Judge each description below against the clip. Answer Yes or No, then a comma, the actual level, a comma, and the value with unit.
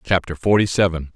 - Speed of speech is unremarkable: Yes, average, 155 wpm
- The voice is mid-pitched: No, very low, 90 Hz